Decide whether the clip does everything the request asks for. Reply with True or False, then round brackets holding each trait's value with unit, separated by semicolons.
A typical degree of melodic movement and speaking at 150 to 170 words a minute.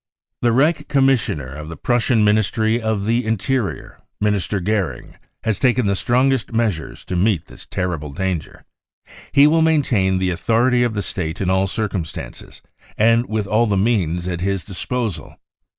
True (4.6 semitones; 160 wpm)